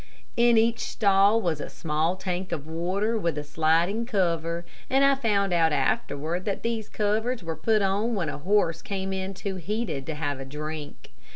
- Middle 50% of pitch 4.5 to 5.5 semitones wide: Yes, average, 4.9 semitones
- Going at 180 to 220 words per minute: Yes, average, 185 wpm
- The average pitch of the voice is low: No, medium, 185 Hz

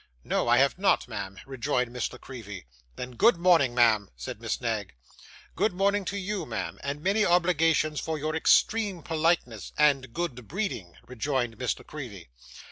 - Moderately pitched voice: Yes, medium, 145 Hz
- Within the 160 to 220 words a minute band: Yes, average, 165 wpm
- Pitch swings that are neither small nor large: No, wide, 6.6 semitones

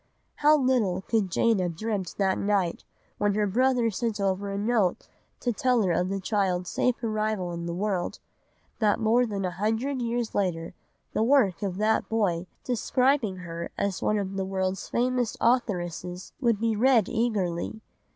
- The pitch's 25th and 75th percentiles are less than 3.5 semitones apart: No, average, 3.9 semitones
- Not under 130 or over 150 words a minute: No, average, 170 wpm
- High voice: Yes, high, 205 Hz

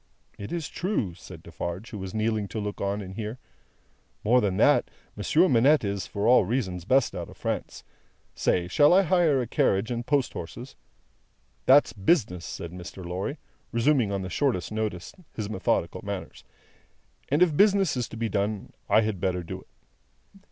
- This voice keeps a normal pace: Yes, average, 175 wpm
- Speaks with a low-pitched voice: Yes, low, 110 Hz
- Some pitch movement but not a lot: No, wide, 5.8 semitones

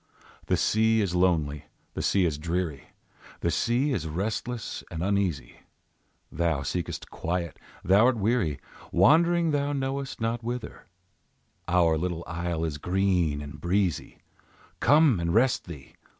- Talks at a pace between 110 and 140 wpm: Yes, slow, 135 wpm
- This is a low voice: Yes, very low, 90 Hz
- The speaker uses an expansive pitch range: Yes, wide, 6.1 semitones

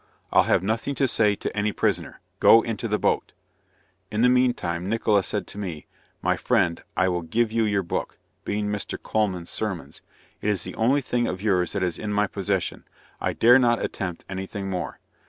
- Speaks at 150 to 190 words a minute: No, average, 200 wpm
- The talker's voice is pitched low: Yes, low, 105 Hz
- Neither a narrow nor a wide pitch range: Yes, average, 3.4 semitones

